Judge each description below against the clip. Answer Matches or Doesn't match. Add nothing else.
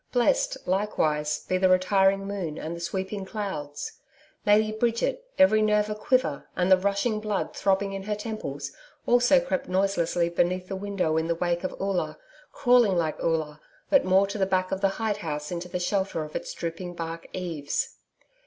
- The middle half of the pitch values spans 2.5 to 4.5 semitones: Matches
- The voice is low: Doesn't match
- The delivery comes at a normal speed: Matches